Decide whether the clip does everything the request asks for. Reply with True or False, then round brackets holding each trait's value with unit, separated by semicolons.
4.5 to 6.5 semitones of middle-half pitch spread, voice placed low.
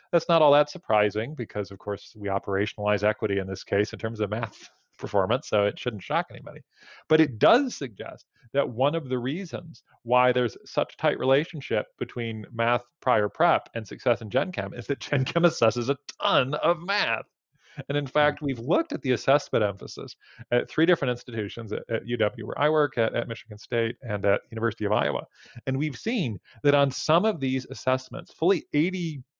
True (5.2 semitones; 125 Hz)